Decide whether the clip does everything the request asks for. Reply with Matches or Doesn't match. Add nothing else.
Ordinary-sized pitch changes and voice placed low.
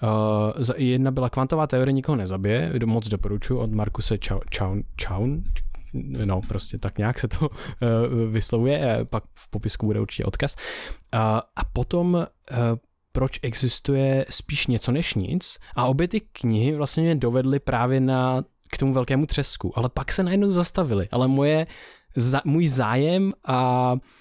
Matches